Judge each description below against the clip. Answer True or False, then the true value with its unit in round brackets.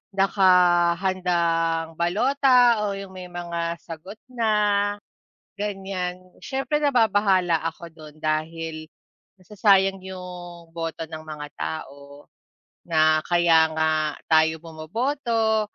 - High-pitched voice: False (175 Hz)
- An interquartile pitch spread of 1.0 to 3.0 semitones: False (3.9 semitones)